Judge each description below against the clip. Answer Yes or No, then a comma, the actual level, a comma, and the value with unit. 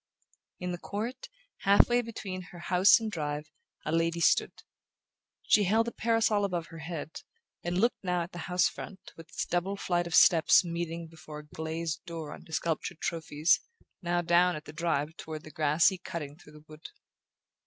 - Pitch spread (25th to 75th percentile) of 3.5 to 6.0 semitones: No, narrow, 2.6 semitones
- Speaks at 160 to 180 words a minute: Yes, average, 175 wpm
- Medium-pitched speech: Yes, medium, 170 Hz